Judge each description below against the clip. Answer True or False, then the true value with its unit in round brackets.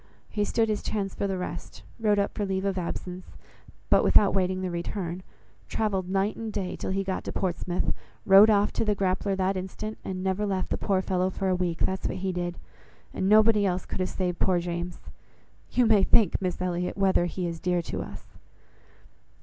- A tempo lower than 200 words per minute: False (205 wpm)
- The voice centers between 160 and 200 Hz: True (190 Hz)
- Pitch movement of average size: False (1.8 semitones)